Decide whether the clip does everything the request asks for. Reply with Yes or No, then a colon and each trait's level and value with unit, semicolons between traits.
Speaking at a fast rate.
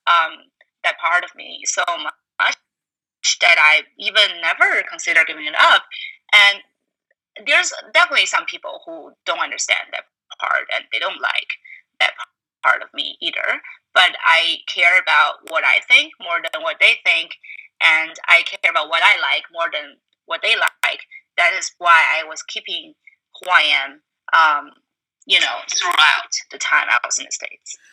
No: average, 165 wpm